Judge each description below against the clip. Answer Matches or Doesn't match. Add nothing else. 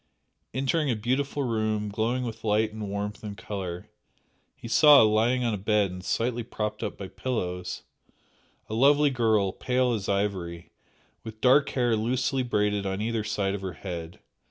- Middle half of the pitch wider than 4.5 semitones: Doesn't match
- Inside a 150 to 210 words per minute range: Matches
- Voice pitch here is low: Matches